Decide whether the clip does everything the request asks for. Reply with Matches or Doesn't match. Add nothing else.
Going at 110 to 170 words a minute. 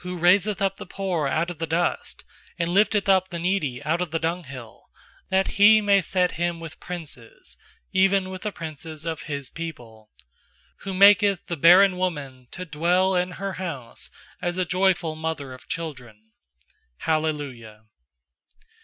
Matches